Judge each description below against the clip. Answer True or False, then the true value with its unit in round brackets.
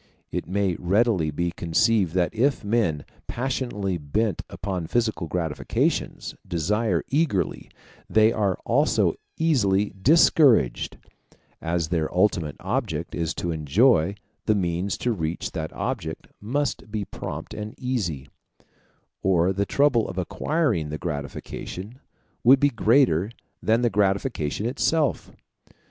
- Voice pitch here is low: True (100 Hz)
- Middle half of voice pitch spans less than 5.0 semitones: False (5.6 semitones)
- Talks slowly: True (120 wpm)